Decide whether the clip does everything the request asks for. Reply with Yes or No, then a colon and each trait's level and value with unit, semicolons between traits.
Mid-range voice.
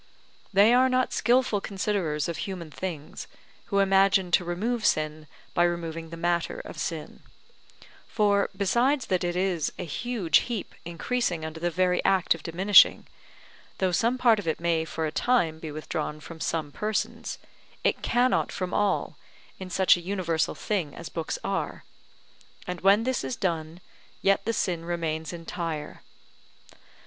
Yes: medium, 180 Hz